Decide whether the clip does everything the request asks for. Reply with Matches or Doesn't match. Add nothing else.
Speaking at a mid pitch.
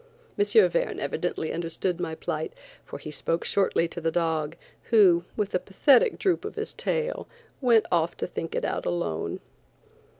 Matches